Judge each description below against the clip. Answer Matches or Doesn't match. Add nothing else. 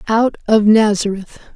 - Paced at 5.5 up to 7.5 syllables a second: Doesn't match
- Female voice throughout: Matches